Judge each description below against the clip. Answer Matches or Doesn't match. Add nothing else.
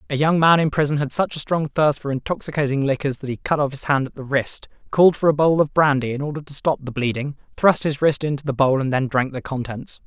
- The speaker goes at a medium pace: Doesn't match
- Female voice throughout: Doesn't match